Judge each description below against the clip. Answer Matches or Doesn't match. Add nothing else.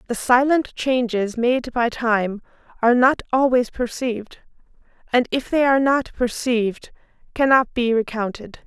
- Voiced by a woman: Matches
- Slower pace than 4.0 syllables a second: Doesn't match